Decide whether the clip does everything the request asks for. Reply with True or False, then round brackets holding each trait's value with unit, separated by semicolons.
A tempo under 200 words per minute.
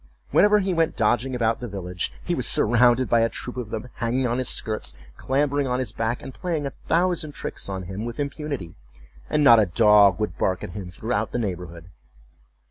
False (205 wpm)